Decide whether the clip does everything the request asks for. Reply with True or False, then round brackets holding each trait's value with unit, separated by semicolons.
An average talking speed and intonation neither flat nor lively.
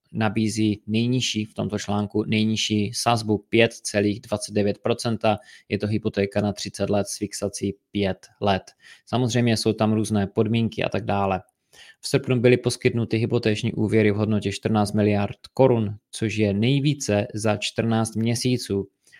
False (135 wpm; 2.0 semitones)